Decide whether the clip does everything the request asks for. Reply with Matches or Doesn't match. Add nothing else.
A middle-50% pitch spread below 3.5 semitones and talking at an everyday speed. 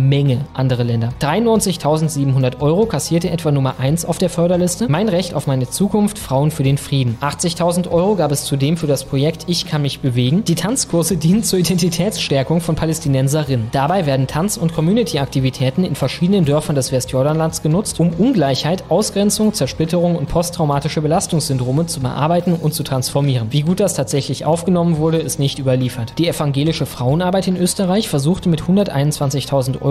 Doesn't match